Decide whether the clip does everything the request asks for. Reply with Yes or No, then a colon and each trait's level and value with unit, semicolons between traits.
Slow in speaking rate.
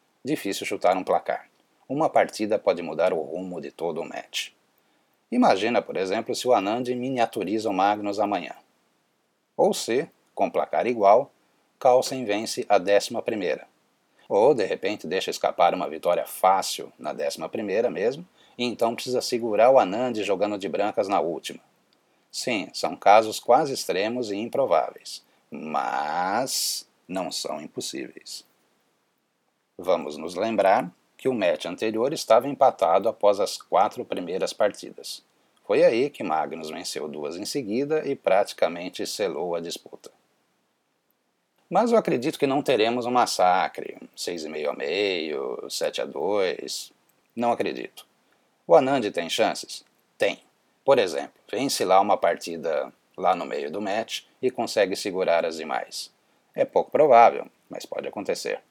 No: average, 140 wpm